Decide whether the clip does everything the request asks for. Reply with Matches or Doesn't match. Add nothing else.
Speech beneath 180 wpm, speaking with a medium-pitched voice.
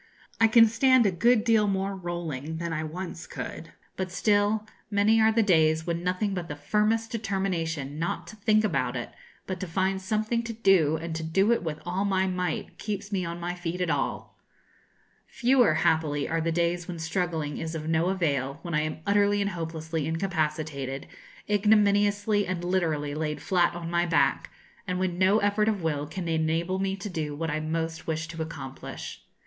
Doesn't match